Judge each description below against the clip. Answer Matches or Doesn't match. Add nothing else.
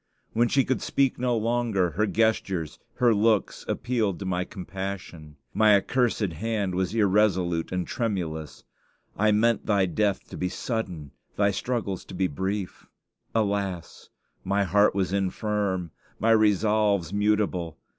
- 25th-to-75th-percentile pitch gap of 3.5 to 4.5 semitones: Doesn't match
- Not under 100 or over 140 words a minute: Matches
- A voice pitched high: Doesn't match